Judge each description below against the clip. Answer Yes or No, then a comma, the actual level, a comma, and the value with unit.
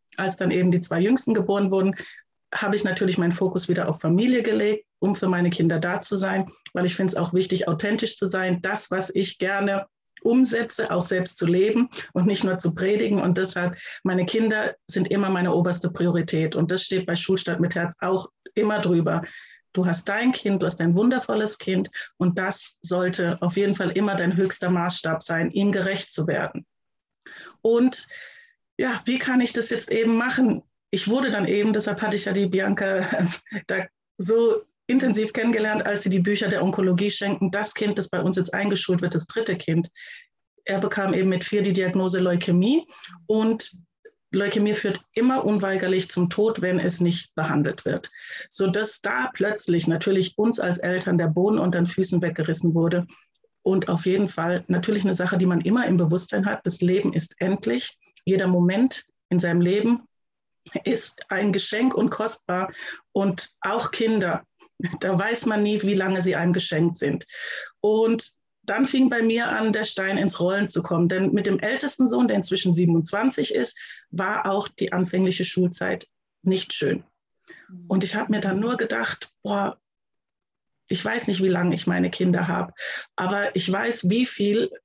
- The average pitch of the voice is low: No, high, 190 Hz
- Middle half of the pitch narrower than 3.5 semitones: Yes, average, 2.9 semitones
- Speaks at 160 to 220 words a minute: Yes, average, 180 wpm